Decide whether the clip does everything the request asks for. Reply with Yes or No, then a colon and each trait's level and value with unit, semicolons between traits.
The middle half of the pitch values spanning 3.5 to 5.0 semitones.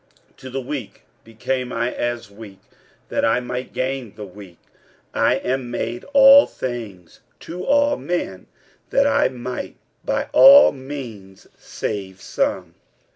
Yes: average, 4.4 semitones